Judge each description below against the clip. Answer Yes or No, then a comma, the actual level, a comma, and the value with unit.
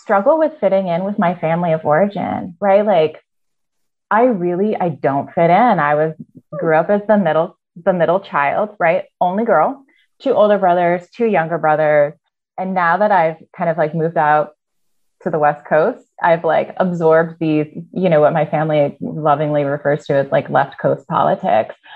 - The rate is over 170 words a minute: Yes, average, 180 wpm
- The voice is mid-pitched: Yes, medium, 170 Hz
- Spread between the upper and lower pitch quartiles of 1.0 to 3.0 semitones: No, average, 4.5 semitones